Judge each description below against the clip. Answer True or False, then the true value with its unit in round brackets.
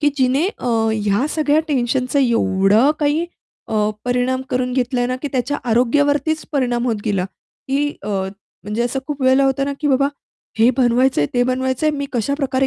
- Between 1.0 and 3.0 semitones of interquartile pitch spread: True (2.7 semitones)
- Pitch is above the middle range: True (260 Hz)